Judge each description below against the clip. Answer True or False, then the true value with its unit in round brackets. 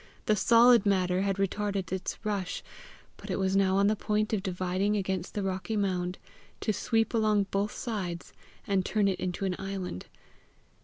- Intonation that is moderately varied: False (2.0 semitones)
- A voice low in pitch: False (195 Hz)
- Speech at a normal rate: True (170 wpm)